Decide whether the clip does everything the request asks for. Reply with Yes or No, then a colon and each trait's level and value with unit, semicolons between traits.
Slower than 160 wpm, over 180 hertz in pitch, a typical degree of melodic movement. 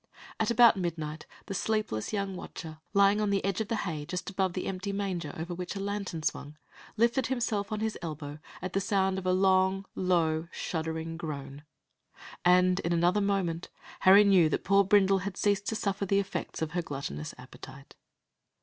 No: average, 185 wpm; high, 190 Hz; average, 3.3 semitones